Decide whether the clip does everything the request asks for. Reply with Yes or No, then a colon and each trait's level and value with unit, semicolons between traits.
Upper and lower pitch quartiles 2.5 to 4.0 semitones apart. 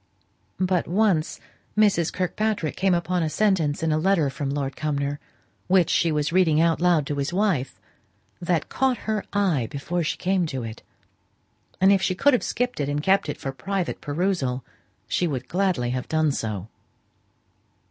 No: average, 4.9 semitones